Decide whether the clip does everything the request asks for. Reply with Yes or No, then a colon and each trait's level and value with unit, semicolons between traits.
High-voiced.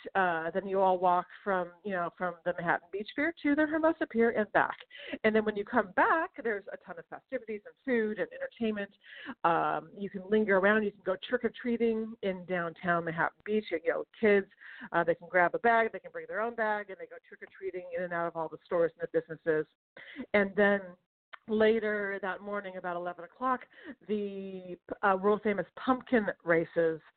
Yes: high, 205 Hz